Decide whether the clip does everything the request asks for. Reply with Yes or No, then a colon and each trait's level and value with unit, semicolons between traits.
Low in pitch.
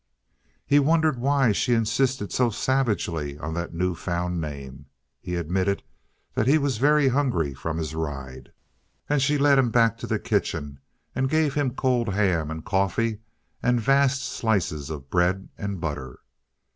Yes: low, 100 Hz